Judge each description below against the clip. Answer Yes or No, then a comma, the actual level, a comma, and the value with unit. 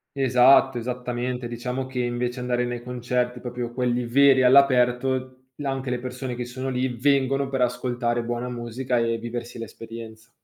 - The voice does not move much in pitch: Yes, narrow, 1.2 semitones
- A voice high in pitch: No, low, 125 Hz